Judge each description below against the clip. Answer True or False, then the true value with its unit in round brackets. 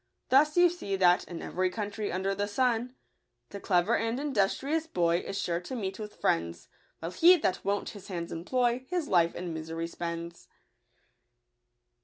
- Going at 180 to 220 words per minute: False (170 wpm)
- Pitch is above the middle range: True (195 Hz)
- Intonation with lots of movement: True (6.2 semitones)